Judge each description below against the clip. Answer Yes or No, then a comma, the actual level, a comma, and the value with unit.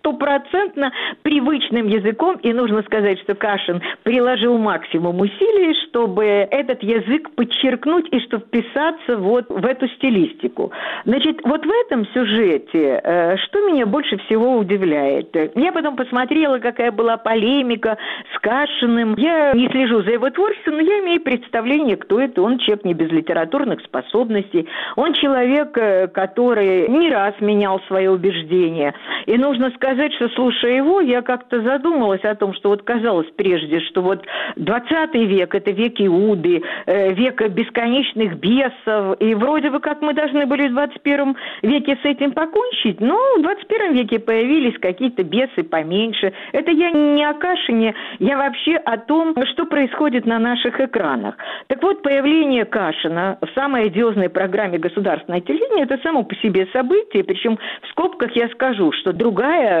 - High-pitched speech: Yes, high, 245 Hz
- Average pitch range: No, wide, 5.7 semitones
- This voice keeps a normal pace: Yes, average, 150 wpm